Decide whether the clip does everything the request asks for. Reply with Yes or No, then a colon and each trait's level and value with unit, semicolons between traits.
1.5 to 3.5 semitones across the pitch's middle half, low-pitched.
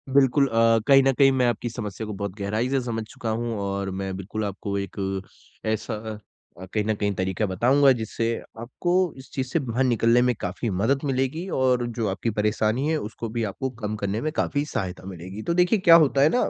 No: average, 4.5 semitones; low, 115 Hz